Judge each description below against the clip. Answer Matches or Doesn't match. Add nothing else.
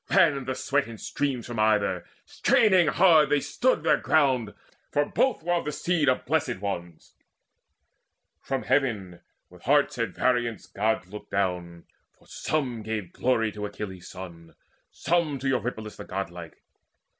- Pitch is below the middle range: Matches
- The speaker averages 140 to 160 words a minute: Matches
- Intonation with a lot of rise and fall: Matches